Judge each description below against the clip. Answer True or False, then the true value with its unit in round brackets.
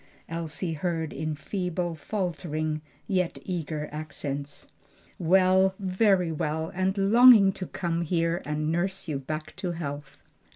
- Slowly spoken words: True (125 wpm)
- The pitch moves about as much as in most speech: True (3.3 semitones)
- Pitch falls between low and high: True (170 Hz)